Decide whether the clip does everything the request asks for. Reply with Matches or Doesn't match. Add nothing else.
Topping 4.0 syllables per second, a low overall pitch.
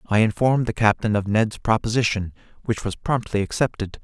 Matches